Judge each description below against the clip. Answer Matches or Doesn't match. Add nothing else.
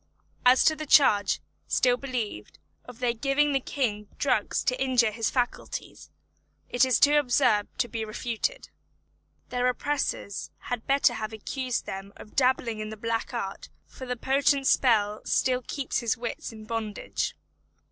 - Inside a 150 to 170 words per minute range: Matches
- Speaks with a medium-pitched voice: Doesn't match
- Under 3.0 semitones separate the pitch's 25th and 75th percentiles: Doesn't match